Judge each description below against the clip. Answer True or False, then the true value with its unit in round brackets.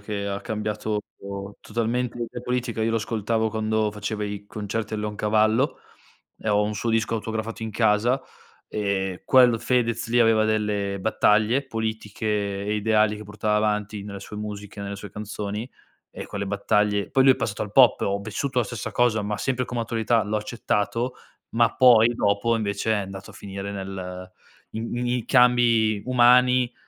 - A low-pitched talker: True (110 Hz)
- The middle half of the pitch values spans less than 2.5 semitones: True (2.0 semitones)